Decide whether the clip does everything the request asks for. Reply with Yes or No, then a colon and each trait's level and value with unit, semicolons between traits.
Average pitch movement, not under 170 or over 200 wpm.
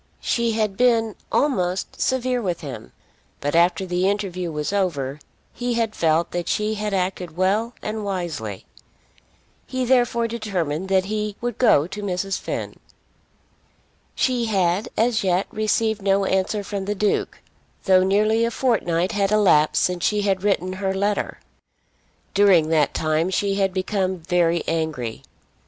No: average, 3.3 semitones; average, 145 wpm